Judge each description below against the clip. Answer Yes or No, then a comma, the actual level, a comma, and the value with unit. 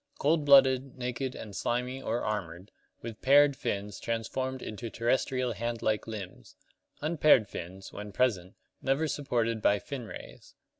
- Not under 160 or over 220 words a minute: No, average, 140 wpm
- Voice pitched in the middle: No, low, 120 Hz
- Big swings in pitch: No, average, 4.0 semitones